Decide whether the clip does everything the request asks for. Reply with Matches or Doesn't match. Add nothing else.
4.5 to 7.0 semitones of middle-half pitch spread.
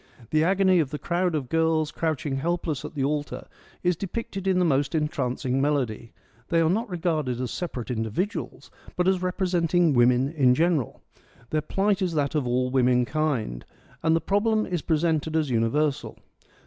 Matches